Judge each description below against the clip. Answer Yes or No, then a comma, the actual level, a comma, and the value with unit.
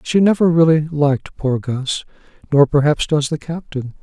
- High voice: No, medium, 150 Hz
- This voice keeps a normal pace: Yes, average, 150 wpm